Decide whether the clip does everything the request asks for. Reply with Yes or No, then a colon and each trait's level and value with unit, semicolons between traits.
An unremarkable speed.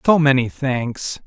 Yes: average, 145 wpm